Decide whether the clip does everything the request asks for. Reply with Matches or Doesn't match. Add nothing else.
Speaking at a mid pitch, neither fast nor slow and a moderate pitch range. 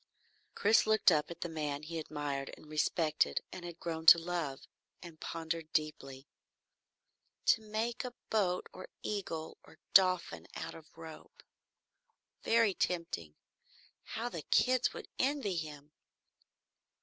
Doesn't match